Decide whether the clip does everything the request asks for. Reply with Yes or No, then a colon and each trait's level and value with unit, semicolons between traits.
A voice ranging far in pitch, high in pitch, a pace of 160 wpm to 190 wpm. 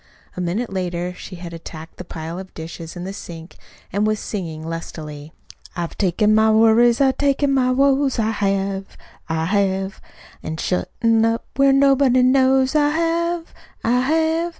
Yes: wide, 7.1 semitones; high, 215 Hz; average, 165 wpm